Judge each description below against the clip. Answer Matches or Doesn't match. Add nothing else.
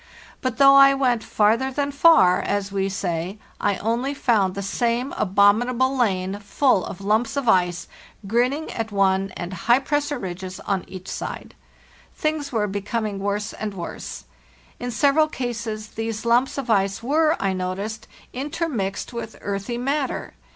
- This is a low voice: Doesn't match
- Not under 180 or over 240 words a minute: Doesn't match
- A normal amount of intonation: Matches